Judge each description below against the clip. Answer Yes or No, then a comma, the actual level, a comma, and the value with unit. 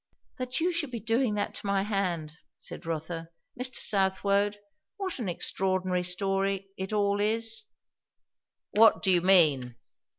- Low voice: No, high, 195 Hz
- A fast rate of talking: No, average, 140 wpm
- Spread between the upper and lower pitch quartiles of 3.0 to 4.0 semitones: Yes, average, 3.5 semitones